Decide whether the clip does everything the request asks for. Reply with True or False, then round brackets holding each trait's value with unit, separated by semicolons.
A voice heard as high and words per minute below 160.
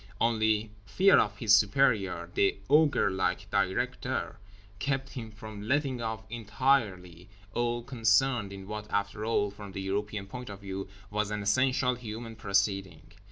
False (105 Hz; 145 wpm)